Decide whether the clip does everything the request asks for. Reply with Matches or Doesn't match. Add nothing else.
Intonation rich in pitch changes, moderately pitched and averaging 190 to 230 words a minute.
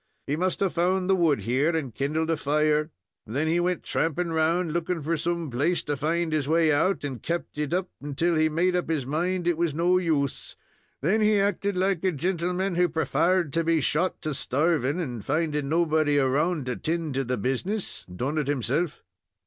Doesn't match